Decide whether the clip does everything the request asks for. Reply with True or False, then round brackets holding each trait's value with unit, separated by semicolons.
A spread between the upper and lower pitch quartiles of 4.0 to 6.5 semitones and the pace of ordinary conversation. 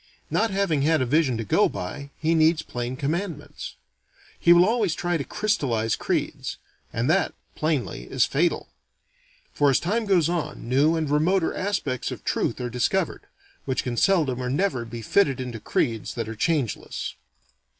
True (5.6 semitones; 165 wpm)